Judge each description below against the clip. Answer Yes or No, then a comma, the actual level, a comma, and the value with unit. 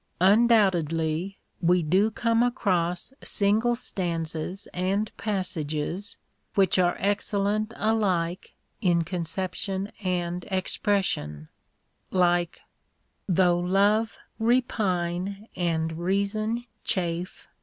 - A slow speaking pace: Yes, slow, 80 wpm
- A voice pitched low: No, medium, 185 Hz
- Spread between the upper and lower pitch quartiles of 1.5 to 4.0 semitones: Yes, average, 3.1 semitones